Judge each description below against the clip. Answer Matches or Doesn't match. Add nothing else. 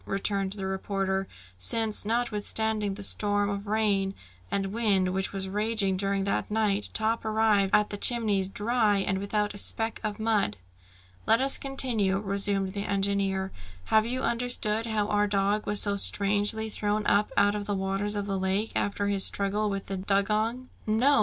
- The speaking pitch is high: Matches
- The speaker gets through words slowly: Doesn't match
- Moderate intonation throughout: Doesn't match